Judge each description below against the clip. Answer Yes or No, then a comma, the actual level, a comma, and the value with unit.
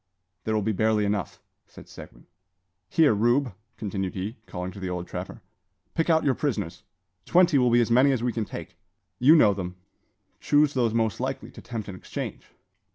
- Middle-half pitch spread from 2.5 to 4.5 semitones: No, average, 4.9 semitones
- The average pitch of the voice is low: Yes, low, 115 Hz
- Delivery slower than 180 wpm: No, average, 185 wpm